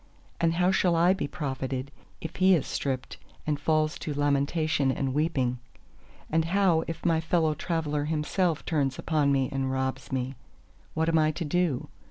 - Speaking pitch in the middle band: Yes, medium, 155 Hz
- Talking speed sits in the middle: Yes, average, 170 wpm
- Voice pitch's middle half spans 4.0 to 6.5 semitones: No, average, 3.2 semitones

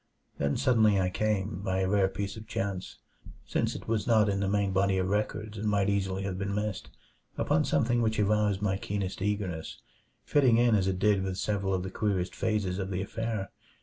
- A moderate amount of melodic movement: No, narrow, 2.0 semitones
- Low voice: Yes, low, 100 Hz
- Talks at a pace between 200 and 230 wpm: Yes, fast, 205 wpm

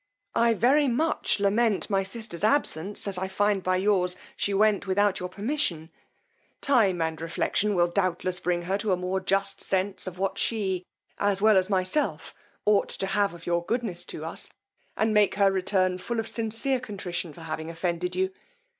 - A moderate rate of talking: Yes, average, 180 wpm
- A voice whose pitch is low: No, high, 195 Hz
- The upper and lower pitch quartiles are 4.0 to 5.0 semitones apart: No, average, 2.7 semitones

